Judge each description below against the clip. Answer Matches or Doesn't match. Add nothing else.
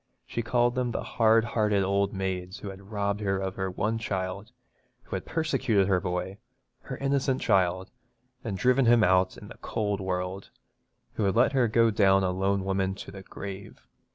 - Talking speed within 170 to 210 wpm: Matches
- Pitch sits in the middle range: Doesn't match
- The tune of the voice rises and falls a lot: Doesn't match